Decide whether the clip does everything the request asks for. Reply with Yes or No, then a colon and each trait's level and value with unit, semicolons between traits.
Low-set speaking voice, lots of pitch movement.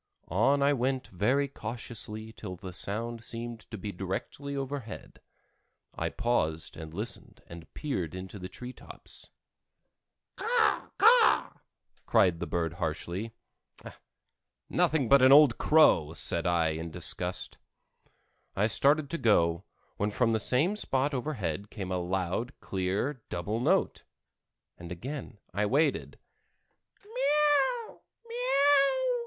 Yes: low, 110 Hz; wide, 6.7 semitones